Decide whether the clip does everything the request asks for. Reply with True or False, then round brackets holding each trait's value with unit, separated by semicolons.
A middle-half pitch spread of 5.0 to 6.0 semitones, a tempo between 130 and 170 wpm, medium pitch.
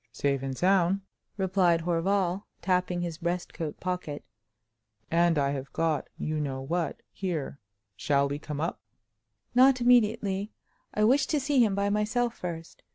True (5.5 semitones; 140 wpm; 175 Hz)